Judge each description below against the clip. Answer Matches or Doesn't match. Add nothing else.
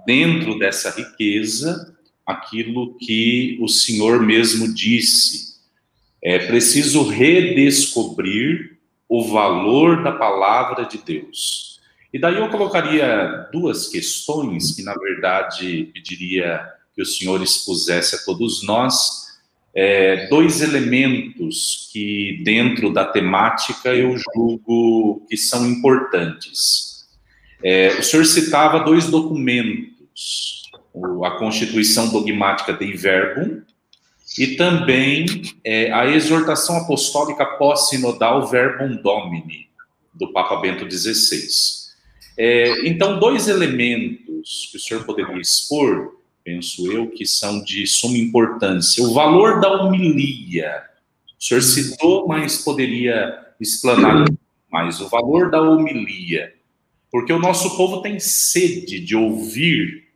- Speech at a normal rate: Doesn't match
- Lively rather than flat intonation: Matches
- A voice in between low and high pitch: Doesn't match